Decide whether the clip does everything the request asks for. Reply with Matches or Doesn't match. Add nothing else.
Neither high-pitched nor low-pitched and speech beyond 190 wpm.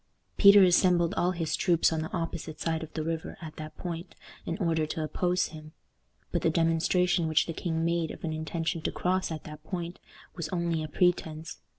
Matches